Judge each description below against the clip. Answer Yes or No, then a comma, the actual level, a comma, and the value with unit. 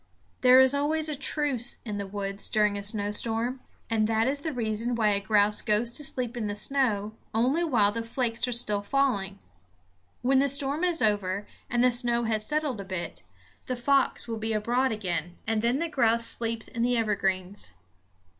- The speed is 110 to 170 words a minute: No, average, 190 wpm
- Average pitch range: Yes, average, 3.8 semitones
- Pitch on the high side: Yes, high, 230 Hz